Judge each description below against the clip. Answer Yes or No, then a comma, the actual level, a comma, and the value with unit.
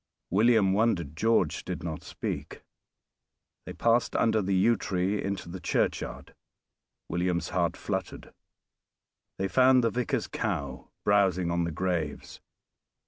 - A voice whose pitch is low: Yes, very low, 95 Hz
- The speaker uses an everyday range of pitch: Yes, average, 4.1 semitones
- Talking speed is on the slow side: Yes, slow, 120 wpm